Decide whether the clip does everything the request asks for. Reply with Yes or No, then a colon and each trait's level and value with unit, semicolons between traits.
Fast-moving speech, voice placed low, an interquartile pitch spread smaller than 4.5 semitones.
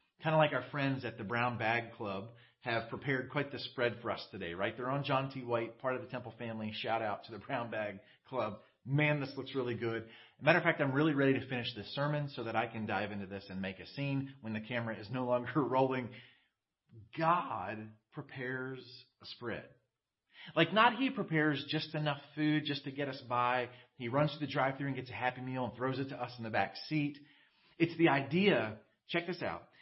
Yes: fast, 225 wpm; low, 130 Hz; average, 3.9 semitones